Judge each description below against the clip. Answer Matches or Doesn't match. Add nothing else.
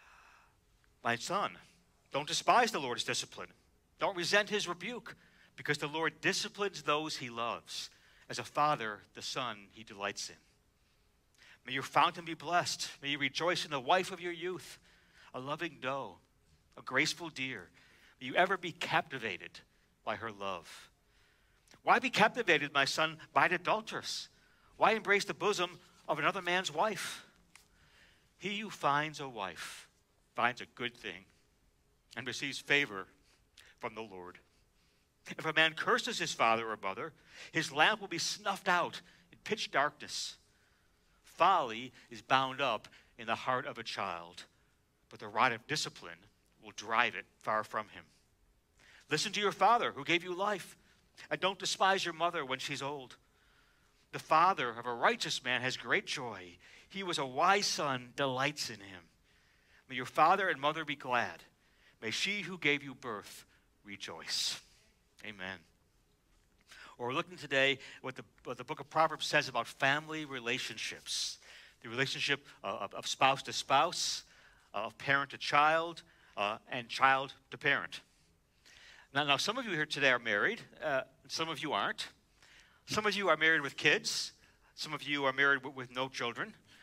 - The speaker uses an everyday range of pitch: Doesn't match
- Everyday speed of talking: Matches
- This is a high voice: Doesn't match